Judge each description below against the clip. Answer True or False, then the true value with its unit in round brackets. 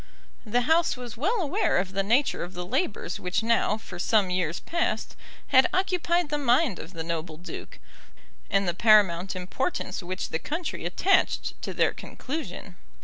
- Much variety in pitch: True (8.6 semitones)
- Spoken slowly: False (165 wpm)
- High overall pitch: True (215 Hz)